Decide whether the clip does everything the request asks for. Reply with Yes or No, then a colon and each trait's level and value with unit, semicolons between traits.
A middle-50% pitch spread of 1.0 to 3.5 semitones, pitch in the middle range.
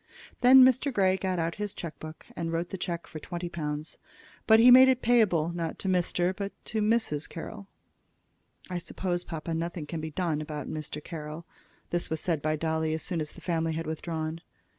Yes: average, 3.1 semitones; medium, 170 Hz